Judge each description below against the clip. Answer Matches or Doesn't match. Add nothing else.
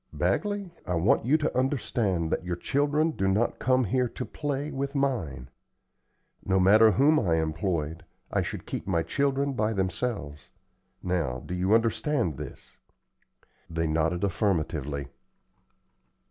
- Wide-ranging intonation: Matches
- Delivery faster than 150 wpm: Doesn't match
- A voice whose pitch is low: Matches